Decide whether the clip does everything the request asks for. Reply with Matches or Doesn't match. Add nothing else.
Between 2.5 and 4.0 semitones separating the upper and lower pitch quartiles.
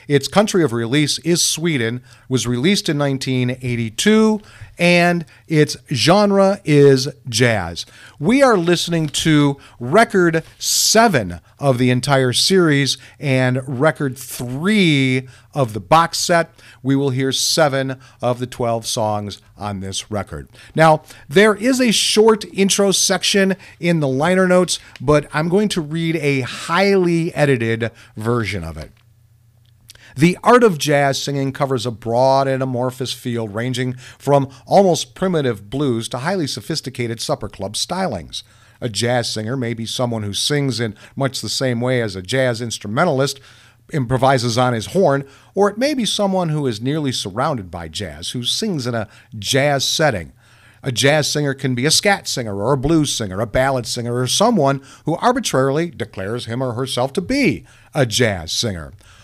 Doesn't match